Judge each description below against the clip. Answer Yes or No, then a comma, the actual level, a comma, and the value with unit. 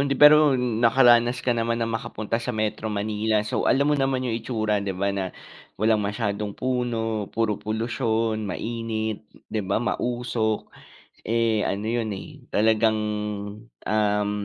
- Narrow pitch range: Yes, narrow, 2.0 semitones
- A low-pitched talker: Yes, low, 110 Hz